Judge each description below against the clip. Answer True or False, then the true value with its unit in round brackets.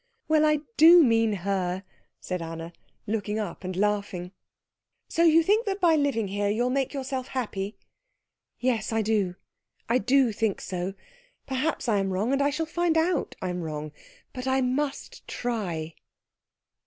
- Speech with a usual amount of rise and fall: False (6.5 semitones)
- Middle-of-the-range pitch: False (225 Hz)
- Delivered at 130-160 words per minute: True (155 wpm)